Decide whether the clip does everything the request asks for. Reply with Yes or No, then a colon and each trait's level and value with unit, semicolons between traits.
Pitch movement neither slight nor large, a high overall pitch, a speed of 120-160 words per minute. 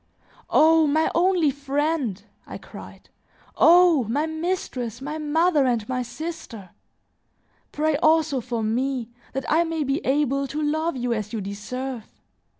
Yes: average, 4.4 semitones; very high, 285 Hz; average, 140 wpm